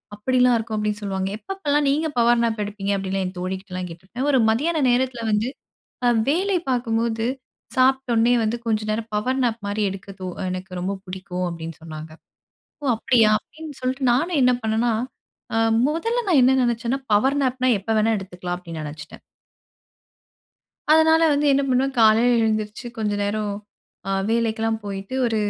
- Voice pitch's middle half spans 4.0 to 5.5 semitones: Yes, average, 4.5 semitones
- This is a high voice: Yes, high, 225 Hz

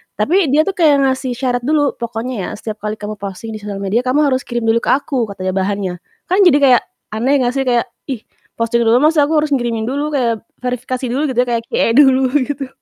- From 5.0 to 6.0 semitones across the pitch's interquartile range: No, average, 3.8 semitones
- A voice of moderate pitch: No, high, 245 Hz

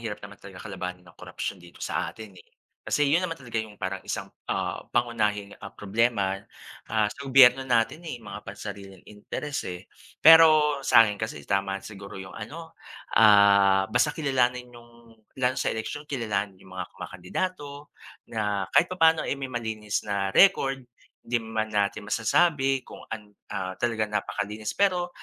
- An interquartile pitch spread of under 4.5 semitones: No, average, 5.1 semitones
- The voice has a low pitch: Yes, low, 110 Hz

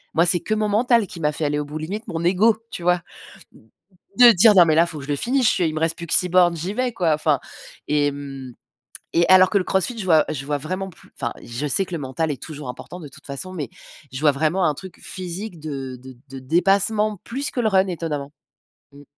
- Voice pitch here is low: No, medium, 170 Hz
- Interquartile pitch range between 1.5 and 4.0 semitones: No, average, 4.6 semitones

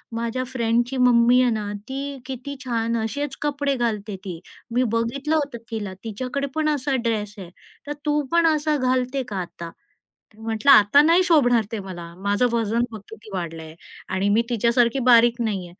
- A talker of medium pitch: No, high, 235 Hz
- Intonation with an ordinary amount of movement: Yes, average, 4.0 semitones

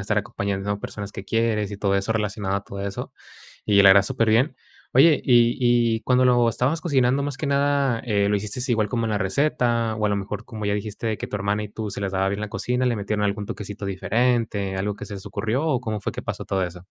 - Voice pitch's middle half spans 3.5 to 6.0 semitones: No, average, 3.1 semitones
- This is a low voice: Yes, low, 105 Hz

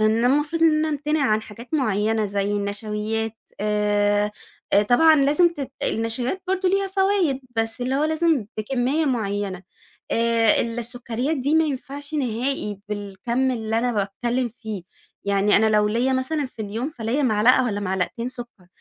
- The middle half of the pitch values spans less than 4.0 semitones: No, average, 4.9 semitones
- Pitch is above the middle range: Yes, high, 235 Hz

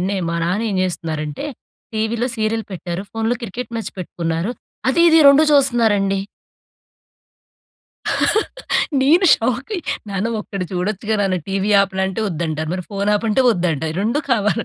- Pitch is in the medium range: No, high, 205 Hz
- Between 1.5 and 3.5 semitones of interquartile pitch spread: No, average, 4.2 semitones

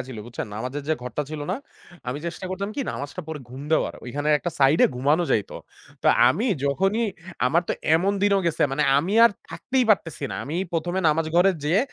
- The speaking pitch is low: No, medium, 160 Hz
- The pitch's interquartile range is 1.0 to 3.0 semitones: No, average, 5.0 semitones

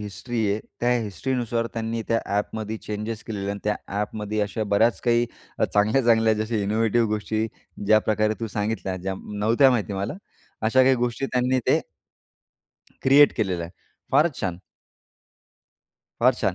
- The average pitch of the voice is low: Yes, low, 110 Hz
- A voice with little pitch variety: Yes, narrow, 2.3 semitones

